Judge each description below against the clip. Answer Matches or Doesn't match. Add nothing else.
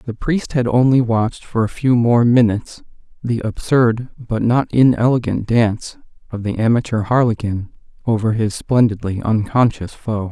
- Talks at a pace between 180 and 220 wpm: Doesn't match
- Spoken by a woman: Doesn't match